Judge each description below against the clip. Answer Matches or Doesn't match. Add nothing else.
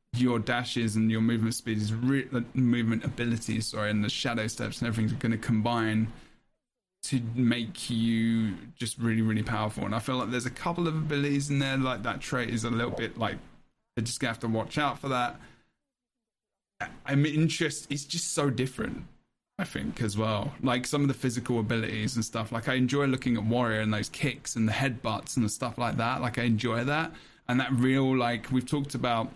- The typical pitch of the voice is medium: Doesn't match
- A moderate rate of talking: Doesn't match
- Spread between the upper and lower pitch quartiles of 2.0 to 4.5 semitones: Matches